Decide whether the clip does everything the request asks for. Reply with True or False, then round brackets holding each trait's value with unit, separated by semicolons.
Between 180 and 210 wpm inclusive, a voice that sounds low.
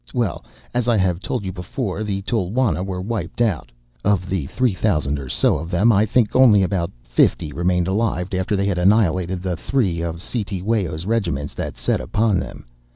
True (185 wpm; 95 Hz)